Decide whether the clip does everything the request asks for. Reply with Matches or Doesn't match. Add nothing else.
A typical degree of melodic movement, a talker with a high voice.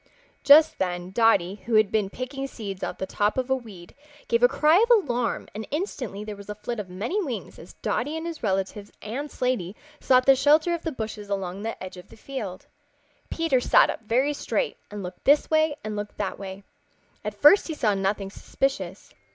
Doesn't match